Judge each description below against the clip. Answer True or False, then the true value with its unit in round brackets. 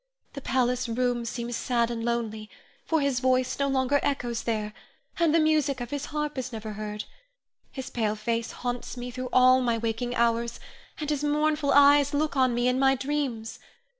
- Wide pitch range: False (3.1 semitones)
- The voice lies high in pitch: True (250 Hz)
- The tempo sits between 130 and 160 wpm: False (185 wpm)